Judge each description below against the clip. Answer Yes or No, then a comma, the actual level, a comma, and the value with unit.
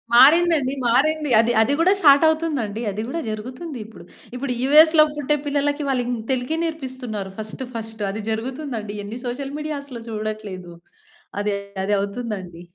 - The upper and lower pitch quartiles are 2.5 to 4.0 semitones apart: No, average, 5.3 semitones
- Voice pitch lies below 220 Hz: No, very high, 250 Hz